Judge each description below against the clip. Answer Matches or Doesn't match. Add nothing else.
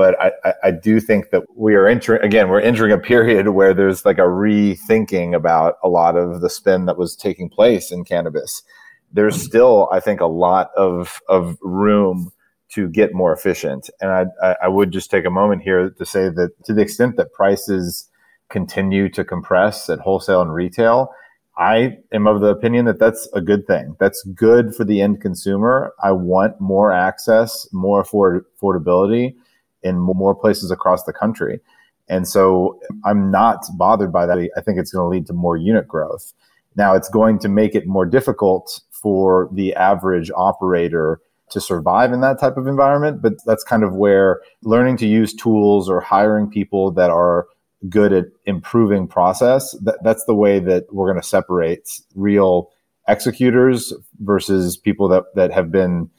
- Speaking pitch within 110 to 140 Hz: Doesn't match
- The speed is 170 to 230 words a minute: Matches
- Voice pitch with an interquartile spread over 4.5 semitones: Doesn't match